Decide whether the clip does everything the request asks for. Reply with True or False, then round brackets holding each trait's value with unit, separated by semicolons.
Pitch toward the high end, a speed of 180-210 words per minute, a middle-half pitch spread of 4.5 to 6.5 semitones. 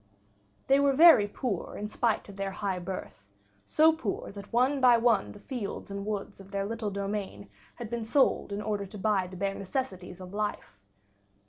False (205 Hz; 190 wpm; 3.3 semitones)